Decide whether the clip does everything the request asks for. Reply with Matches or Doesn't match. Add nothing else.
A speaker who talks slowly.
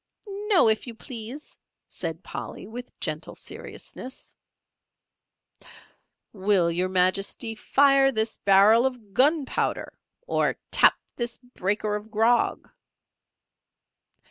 Matches